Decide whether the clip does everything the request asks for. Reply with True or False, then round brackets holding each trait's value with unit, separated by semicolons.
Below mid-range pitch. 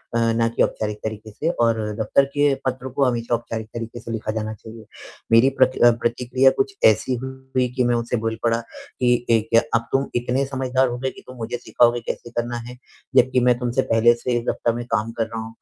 True (120 Hz)